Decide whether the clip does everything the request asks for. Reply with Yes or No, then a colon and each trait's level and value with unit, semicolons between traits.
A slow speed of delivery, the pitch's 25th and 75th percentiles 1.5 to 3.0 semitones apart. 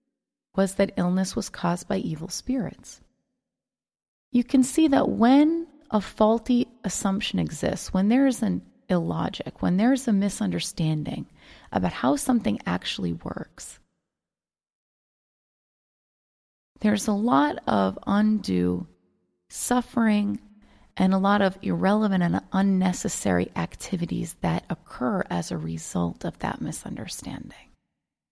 No: slow, 110 wpm; average, 5.3 semitones